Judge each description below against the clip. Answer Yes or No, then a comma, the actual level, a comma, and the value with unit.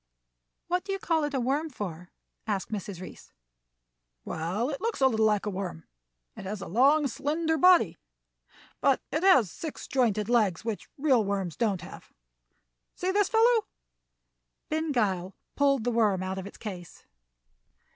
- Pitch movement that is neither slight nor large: No, wide, 7.9 semitones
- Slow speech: No, average, 160 wpm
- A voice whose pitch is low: No, high, 235 Hz